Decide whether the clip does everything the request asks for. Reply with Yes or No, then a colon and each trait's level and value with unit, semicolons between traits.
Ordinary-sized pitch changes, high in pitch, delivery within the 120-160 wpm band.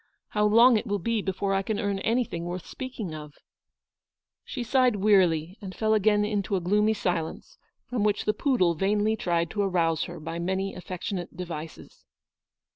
No: average, 3.5 semitones; high, 195 Hz; average, 175 wpm